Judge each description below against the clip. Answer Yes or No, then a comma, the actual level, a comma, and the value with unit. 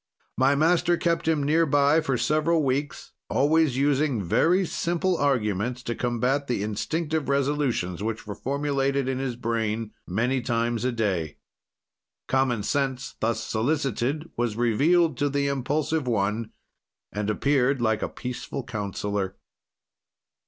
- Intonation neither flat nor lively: Yes, average, 4.4 semitones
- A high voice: No, low, 130 Hz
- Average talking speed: No, slow, 130 wpm